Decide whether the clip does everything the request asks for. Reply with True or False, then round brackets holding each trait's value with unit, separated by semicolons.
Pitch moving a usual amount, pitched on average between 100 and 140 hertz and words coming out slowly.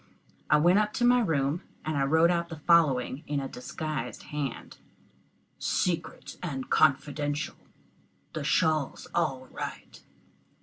False (3.5 semitones; 155 Hz; 125 wpm)